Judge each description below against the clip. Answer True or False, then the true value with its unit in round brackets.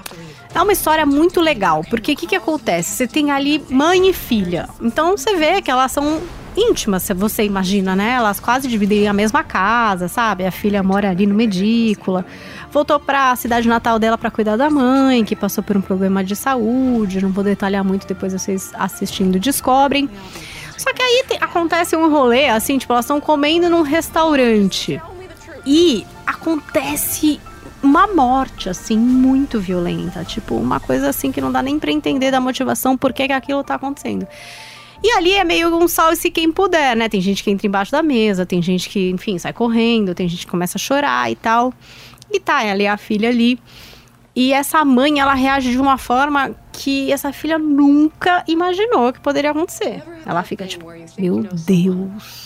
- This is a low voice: False (245 Hz)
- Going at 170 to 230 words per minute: True (185 wpm)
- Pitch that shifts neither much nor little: False (6.9 semitones)